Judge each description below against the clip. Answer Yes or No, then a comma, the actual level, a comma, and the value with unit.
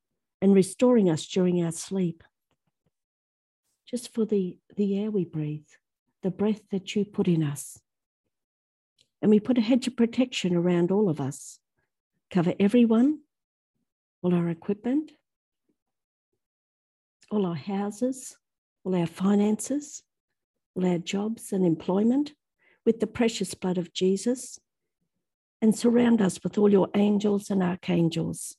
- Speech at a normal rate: No, slow, 130 wpm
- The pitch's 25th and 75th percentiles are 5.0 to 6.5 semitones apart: No, average, 4.3 semitones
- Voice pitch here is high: Yes, high, 200 Hz